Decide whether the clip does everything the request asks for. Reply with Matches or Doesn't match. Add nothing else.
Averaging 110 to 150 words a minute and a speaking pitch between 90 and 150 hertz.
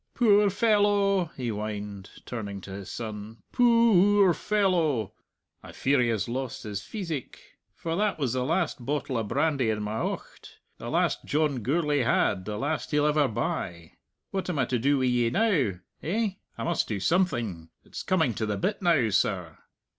Doesn't match